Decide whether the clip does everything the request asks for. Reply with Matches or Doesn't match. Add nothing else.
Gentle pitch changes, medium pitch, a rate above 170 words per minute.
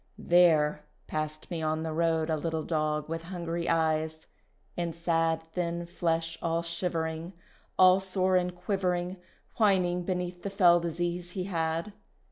Doesn't match